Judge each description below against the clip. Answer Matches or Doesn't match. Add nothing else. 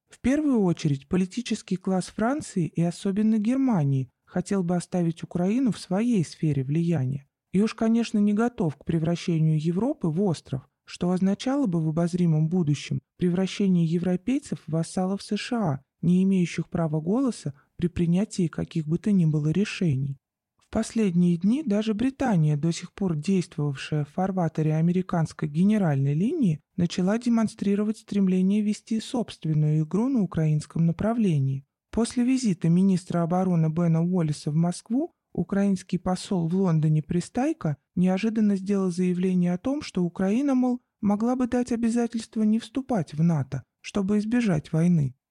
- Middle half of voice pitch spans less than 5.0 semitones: Matches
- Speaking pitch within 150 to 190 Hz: Matches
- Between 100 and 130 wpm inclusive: Doesn't match